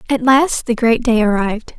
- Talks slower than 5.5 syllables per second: Yes, 5.1 syllables/s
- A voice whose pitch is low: No, high, 235 Hz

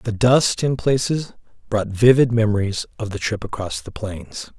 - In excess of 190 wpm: No, average, 170 wpm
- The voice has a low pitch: Yes, low, 110 Hz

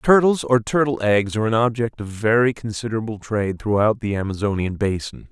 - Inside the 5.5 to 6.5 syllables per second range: Yes, 5.7 syllables/s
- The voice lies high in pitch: No, low, 110 Hz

